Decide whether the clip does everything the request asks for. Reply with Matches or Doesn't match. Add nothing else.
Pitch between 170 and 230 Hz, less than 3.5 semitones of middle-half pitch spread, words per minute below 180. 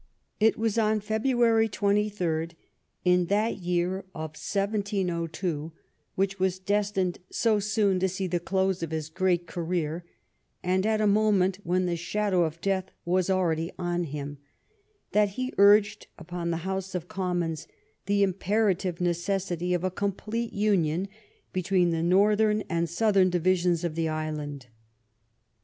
Matches